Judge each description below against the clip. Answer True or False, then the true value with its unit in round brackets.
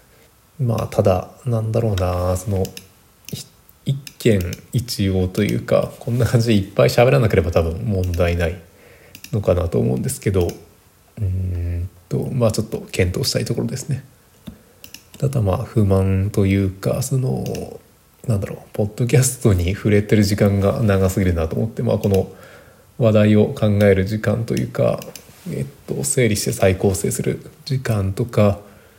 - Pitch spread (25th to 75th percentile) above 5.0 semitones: False (3.5 semitones)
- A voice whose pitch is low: True (100 Hz)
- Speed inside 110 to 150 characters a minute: False (300 characters per minute)